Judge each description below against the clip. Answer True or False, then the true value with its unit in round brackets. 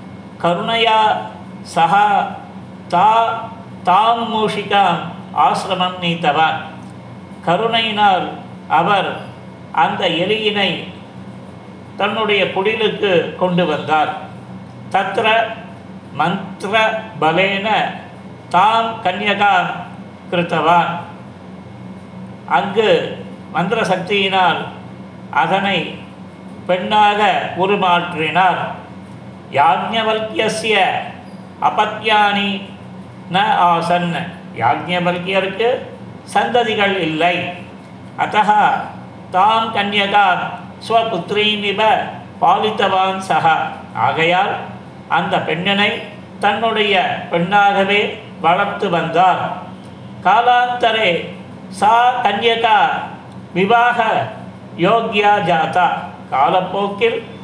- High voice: True (200 Hz)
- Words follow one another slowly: True (55 wpm)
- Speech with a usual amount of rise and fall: True (3.8 semitones)